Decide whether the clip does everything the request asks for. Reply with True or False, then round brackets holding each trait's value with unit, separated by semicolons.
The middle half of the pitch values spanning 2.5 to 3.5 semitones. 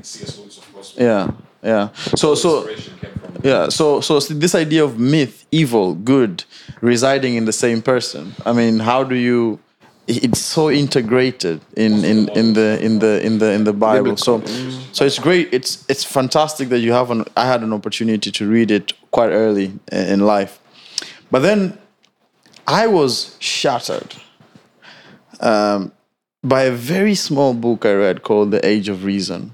False (4.0 semitones)